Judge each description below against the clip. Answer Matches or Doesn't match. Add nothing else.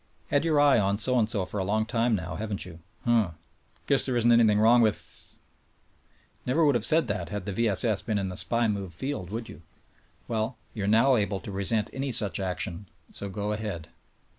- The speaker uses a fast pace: Matches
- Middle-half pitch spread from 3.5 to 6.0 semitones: Doesn't match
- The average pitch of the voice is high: Doesn't match